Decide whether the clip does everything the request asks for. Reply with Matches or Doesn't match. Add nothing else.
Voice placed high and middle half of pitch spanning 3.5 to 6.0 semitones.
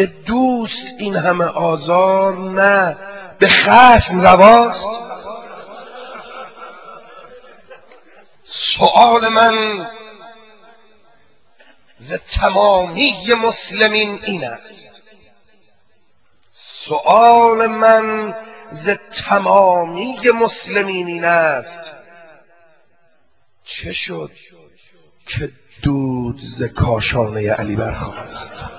Matches